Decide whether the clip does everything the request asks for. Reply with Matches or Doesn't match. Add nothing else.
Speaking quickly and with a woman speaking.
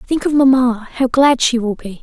Matches